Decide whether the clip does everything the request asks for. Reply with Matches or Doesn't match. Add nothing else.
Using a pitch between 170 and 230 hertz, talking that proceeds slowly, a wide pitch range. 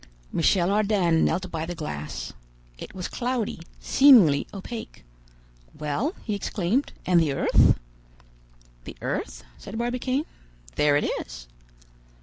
Matches